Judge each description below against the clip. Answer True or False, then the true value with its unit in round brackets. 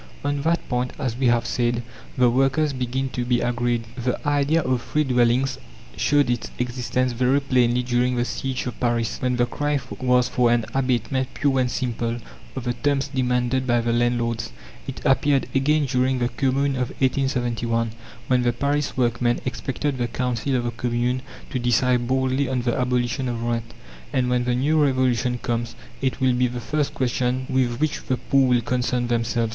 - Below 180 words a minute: False (185 wpm)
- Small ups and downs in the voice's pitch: True (1.7 semitones)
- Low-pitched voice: True (125 Hz)